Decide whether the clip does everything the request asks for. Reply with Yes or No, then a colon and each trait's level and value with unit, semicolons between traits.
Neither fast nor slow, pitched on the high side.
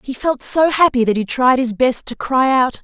No: fast, 255 wpm; very high, 260 Hz